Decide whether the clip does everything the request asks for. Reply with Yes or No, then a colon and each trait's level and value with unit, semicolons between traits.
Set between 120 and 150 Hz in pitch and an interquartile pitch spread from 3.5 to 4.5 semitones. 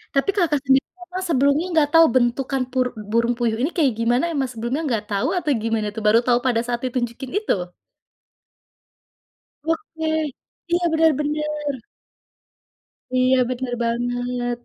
No: very high, 255 Hz; average, 3.9 semitones